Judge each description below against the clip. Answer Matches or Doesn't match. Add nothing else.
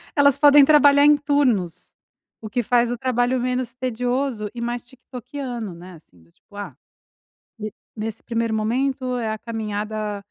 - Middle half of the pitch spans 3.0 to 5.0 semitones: Matches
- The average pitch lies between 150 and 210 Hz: Doesn't match